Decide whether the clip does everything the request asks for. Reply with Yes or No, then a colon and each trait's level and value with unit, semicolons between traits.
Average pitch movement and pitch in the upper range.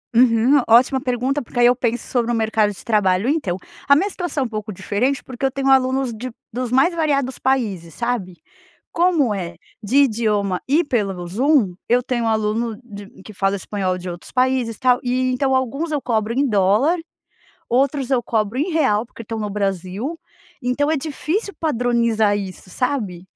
Yes: average, 4.3 semitones; high, 240 Hz